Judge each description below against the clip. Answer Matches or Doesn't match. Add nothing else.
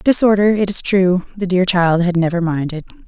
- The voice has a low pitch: Doesn't match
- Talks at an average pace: Matches